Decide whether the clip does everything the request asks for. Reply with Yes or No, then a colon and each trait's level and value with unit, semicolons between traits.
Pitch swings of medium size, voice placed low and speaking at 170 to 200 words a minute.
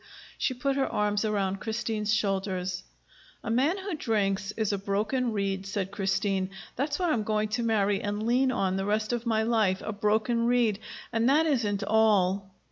No: average, 3.1 semitones; high, 215 Hz; average, 180 wpm